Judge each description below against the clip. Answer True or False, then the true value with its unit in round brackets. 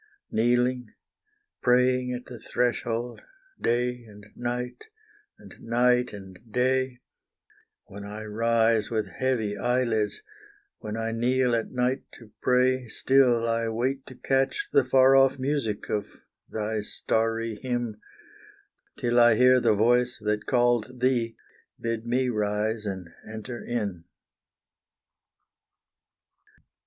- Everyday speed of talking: False (115 wpm)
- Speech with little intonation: True (2.3 semitones)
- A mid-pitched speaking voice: False (120 Hz)